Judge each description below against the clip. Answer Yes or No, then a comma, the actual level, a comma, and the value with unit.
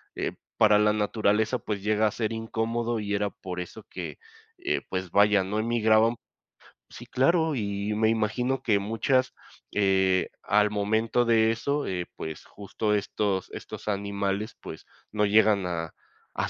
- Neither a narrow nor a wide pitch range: No, narrow, 2.0 semitones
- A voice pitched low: Yes, low, 105 Hz